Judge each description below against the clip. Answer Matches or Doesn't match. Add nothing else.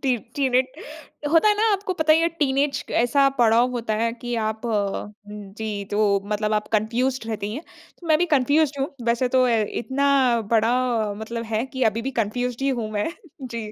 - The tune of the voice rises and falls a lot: Doesn't match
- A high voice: Matches